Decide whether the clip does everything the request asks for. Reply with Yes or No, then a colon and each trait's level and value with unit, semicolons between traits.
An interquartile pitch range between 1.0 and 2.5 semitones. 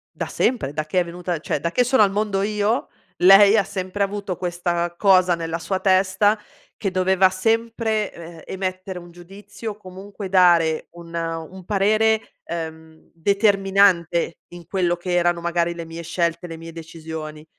No: average, 2.9 semitones